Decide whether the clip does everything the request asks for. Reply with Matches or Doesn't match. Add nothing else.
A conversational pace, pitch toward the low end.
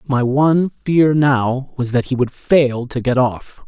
Matches